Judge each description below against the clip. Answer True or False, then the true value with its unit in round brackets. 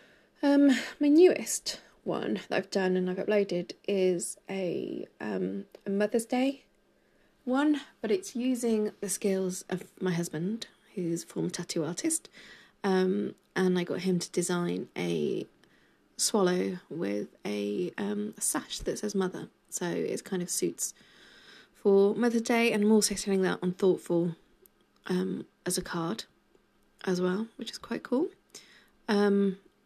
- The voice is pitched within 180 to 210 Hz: True (190 Hz)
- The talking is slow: False (145 wpm)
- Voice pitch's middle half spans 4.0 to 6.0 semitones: False (3.6 semitones)